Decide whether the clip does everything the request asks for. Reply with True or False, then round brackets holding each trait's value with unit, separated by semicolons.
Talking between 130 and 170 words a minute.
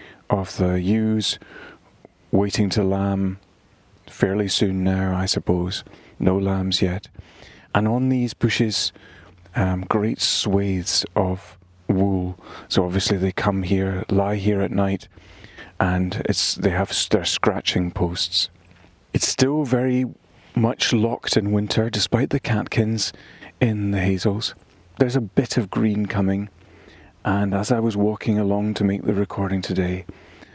True (135 wpm)